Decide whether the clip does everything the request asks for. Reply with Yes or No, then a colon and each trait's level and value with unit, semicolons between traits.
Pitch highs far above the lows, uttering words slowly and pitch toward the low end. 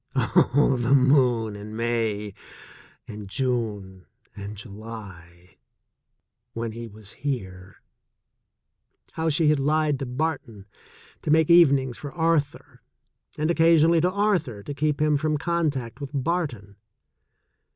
Yes: wide, 6.2 semitones; slow, 120 wpm; low, 130 Hz